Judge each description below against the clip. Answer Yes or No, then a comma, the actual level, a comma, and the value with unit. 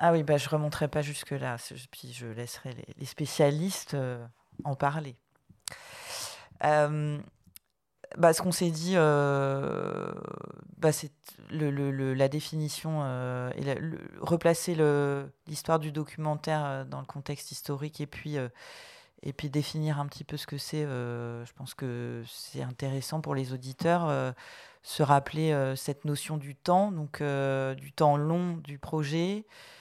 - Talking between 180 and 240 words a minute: No, average, 160 wpm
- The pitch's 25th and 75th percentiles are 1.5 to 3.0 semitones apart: Yes, narrow, 2.6 semitones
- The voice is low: No, medium, 150 Hz